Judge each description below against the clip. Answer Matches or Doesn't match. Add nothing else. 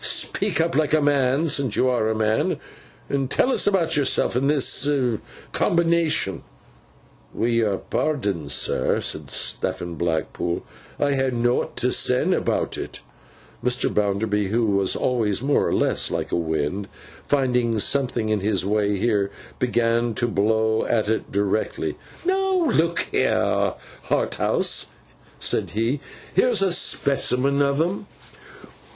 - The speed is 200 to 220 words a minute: Doesn't match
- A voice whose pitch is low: Matches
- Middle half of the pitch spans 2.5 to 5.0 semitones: Doesn't match